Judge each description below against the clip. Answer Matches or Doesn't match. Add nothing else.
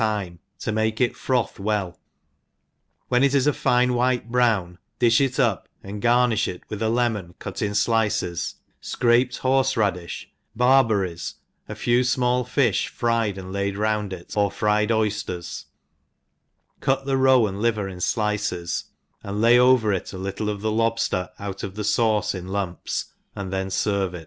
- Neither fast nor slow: Matches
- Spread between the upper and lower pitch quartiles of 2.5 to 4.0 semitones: Matches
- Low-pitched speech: Matches